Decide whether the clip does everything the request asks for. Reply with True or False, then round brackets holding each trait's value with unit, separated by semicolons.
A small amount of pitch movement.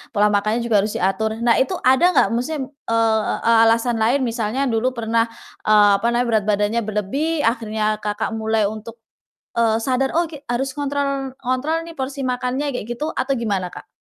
False (3.5 semitones)